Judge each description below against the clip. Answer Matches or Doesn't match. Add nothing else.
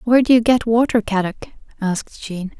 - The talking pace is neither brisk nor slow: Matches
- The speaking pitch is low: Doesn't match